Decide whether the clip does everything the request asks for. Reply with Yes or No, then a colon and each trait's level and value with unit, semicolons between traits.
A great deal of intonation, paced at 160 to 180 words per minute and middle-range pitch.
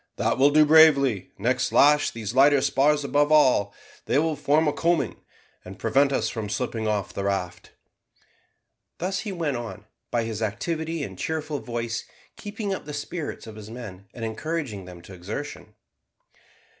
No: wide, 6.0 semitones; average, 165 wpm; low, 130 Hz